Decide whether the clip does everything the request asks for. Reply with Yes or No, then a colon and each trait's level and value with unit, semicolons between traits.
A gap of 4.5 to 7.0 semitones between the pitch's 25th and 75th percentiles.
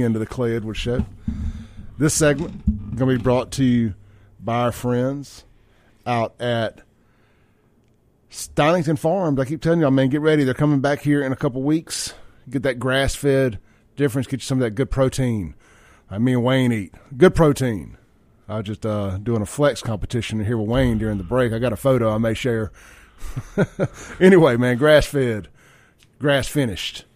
No: average, 4.1 semitones